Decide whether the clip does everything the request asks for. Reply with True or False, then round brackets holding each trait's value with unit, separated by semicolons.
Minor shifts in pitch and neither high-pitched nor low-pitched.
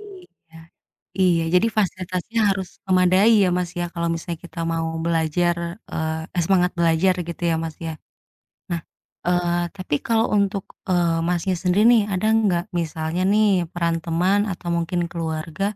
True (2.2 semitones; 175 Hz)